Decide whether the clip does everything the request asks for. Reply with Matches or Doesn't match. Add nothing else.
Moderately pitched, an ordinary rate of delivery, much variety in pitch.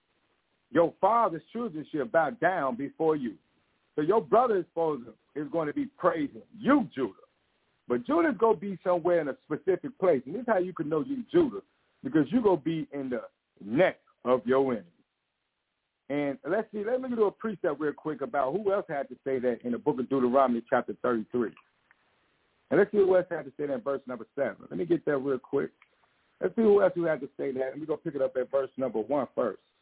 Doesn't match